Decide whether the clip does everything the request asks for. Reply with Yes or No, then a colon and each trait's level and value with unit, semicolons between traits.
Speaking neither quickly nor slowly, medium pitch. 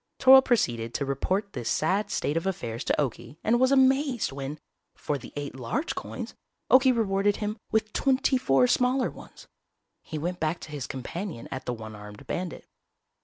Yes: average, 175 wpm; medium, 175 Hz